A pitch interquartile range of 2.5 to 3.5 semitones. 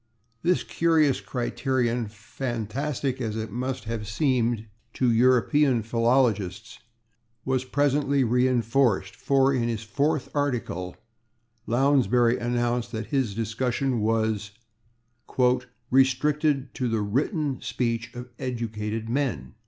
Yes: average, 3.1 semitones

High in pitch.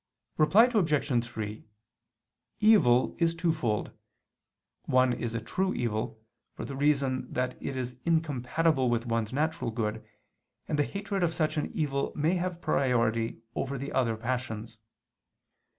No: low, 130 Hz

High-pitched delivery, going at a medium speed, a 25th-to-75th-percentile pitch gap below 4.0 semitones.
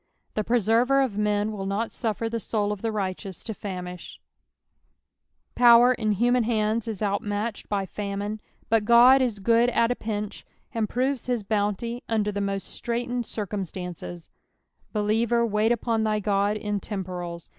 Yes: high, 215 Hz; average, 155 wpm; narrow, 2.5 semitones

